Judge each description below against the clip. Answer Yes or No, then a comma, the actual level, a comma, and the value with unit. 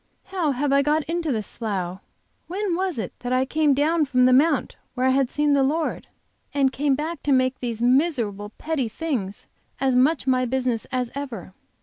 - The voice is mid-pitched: No, very high, 265 Hz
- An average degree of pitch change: Yes, average, 3.4 semitones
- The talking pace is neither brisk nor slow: Yes, average, 195 wpm